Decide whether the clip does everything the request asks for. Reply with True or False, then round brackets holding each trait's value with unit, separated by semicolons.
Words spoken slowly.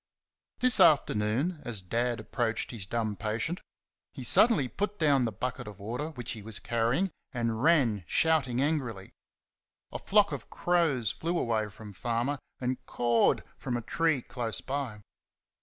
False (150 wpm)